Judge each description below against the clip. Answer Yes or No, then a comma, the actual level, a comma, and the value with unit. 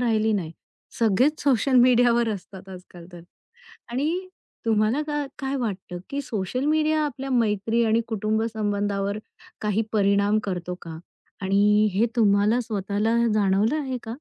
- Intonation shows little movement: No, average, 3.7 semitones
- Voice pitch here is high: Yes, high, 220 Hz